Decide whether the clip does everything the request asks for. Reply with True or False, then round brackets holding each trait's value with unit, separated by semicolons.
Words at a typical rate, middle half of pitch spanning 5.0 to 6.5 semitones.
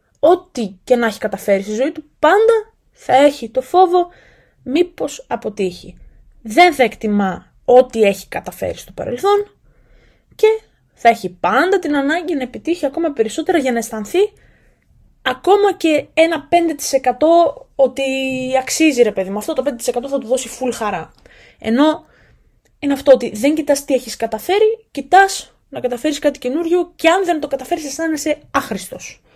True (150 wpm; 5.5 semitones)